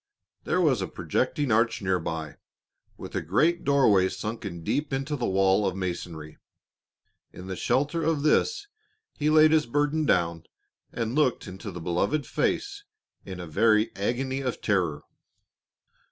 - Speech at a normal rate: Yes, average, 150 wpm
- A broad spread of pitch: Yes, wide, 8.0 semitones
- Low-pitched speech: Yes, low, 110 Hz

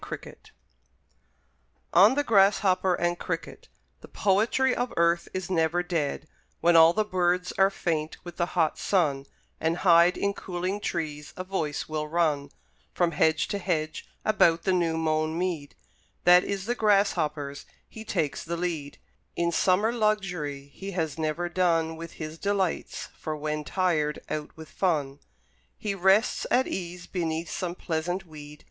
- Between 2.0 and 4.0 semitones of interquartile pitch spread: Yes, average, 3.3 semitones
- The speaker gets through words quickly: No, average, 155 wpm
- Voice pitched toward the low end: No, medium, 175 Hz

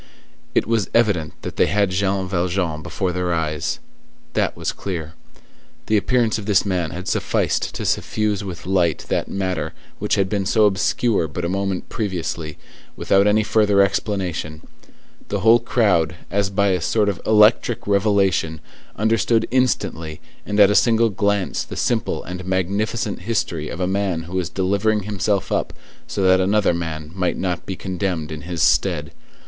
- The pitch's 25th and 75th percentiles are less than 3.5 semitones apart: Yes, average, 2.8 semitones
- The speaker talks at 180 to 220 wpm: No, average, 165 wpm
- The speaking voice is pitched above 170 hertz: No, very low, 95 Hz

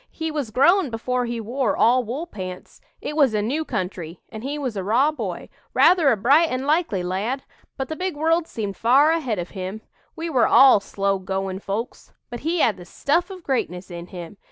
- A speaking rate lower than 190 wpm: No, fast, 205 wpm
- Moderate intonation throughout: No, wide, 7.2 semitones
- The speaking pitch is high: Yes, high, 245 Hz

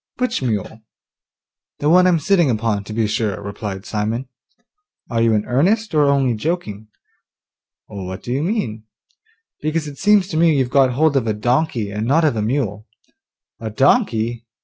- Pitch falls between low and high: No, low, 120 Hz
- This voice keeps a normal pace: Yes, average, 170 wpm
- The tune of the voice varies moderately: No, wide, 6.2 semitones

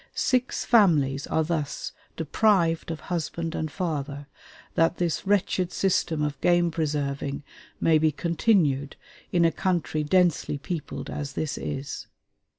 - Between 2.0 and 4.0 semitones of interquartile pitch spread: Yes, average, 3.2 semitones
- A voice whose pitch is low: No, medium, 160 Hz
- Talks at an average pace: No, slow, 130 wpm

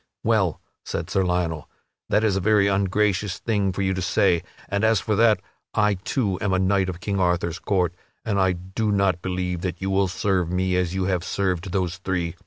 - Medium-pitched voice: No, very low, 95 Hz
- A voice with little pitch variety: Yes, narrow, 1.8 semitones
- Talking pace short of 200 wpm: No, fast, 205 wpm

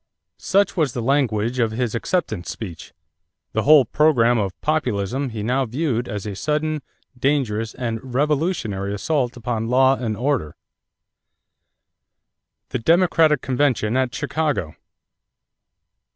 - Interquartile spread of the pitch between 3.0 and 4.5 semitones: No, average, 5.1 semitones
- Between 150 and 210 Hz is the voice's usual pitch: No, low, 125 Hz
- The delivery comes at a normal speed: No, slow, 120 wpm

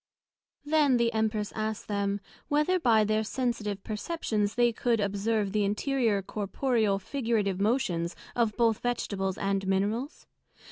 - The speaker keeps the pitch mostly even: No, average, 3.1 semitones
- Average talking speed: No, slow, 130 wpm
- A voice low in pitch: No, high, 215 Hz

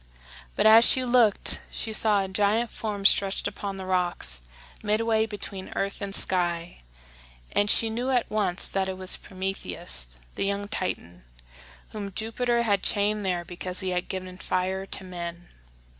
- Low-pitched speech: No, high, 195 Hz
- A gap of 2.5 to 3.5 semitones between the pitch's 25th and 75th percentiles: Yes, average, 2.8 semitones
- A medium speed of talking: Yes, average, 160 wpm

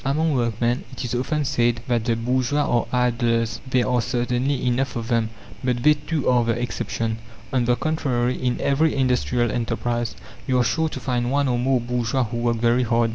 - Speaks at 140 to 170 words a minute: No, average, 195 wpm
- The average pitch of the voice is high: No, low, 120 Hz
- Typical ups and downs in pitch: No, narrow, 1.7 semitones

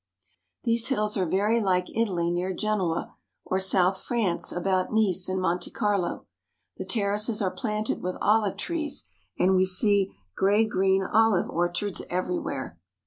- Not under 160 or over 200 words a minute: No, average, 140 wpm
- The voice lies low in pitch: No, high, 195 Hz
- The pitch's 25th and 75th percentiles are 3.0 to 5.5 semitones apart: No, narrow, 2.6 semitones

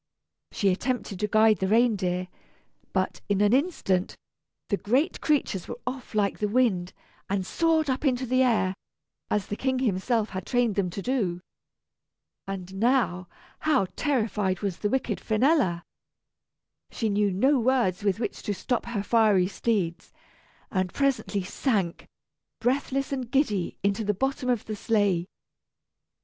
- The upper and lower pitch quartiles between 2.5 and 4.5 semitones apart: No, average, 5.0 semitones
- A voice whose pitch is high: Yes, high, 215 Hz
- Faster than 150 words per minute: No, average, 145 wpm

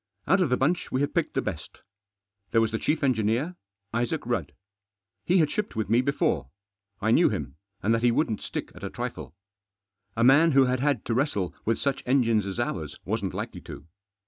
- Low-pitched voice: Yes, low, 120 Hz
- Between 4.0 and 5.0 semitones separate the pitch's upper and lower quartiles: Yes, average, 4.3 semitones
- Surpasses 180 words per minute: Yes, average, 200 wpm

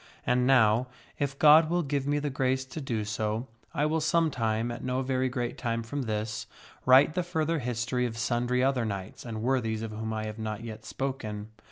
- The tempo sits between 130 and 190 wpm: No, fast, 205 wpm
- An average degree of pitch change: Yes, average, 3.6 semitones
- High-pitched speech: No, low, 125 Hz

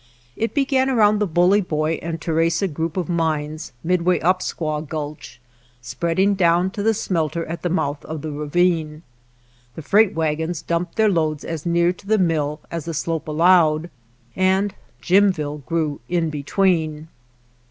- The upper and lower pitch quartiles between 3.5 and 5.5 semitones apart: No, average, 3.0 semitones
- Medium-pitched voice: Yes, medium, 165 Hz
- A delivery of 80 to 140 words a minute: No, average, 155 wpm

